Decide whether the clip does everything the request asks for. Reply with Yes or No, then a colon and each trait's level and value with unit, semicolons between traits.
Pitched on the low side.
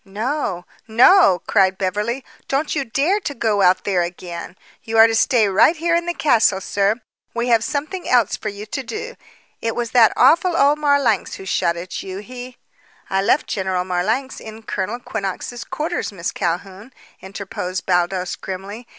No: high, 220 Hz